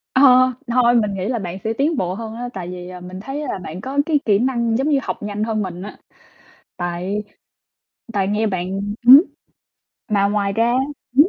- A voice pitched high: Yes, high, 210 Hz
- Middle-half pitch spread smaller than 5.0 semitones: Yes, average, 4.4 semitones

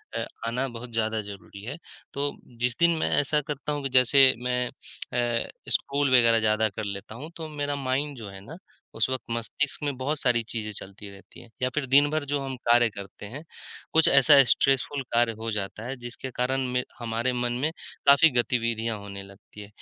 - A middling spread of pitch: Yes, average, 3.8 semitones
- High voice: No, low, 125 Hz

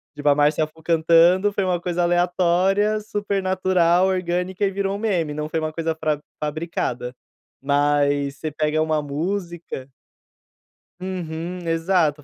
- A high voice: No, medium, 170 Hz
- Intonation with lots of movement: No, average, 3.3 semitones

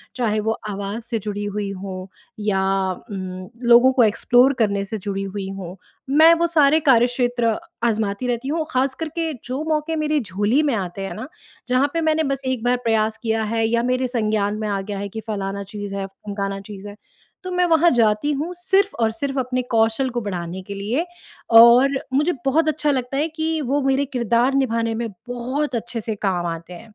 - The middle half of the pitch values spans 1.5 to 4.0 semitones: No, average, 5.0 semitones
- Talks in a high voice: Yes, high, 230 Hz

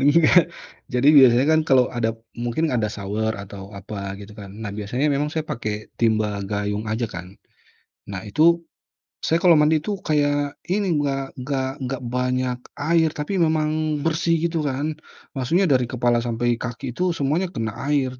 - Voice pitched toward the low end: Yes, low, 130 Hz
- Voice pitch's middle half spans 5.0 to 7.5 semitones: Yes, average, 5.3 semitones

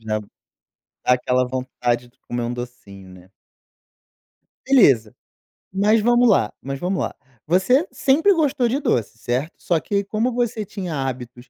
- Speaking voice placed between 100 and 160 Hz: Yes, medium, 140 Hz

